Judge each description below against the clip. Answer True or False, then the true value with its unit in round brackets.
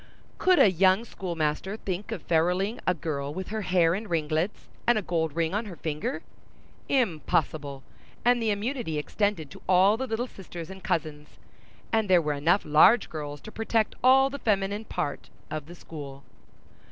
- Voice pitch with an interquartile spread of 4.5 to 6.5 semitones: True (5.5 semitones)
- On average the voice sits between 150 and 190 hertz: True (185 Hz)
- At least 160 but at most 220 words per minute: True (165 wpm)